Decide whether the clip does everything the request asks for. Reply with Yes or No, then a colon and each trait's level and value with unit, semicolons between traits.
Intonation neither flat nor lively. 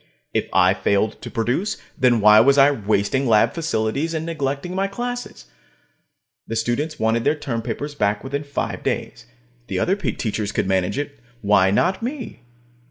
No: wide, 6.3 semitones